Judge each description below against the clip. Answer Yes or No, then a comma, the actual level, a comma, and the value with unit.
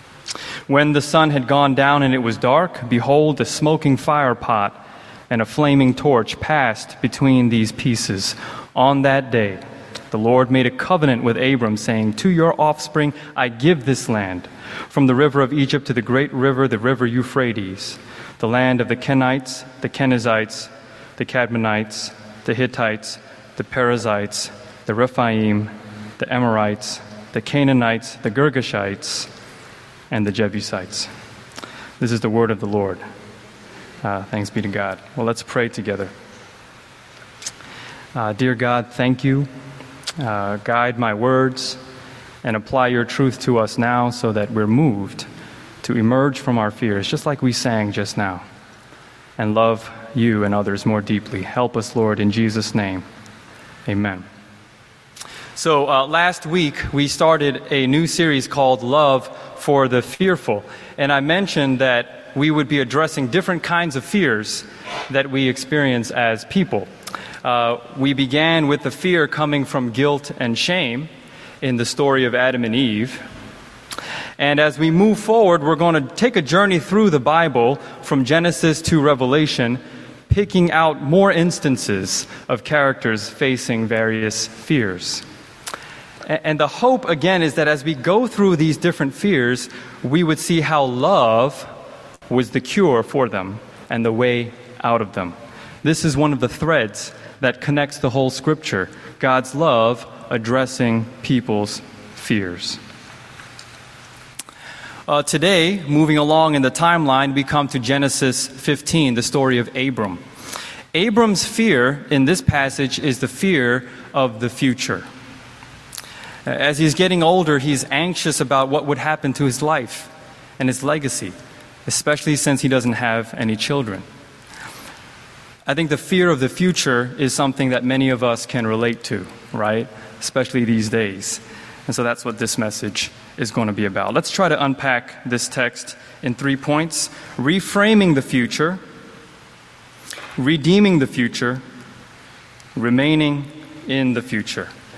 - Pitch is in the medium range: No, low, 130 Hz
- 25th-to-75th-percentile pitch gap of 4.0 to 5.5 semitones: Yes, average, 4.4 semitones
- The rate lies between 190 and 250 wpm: No, average, 150 wpm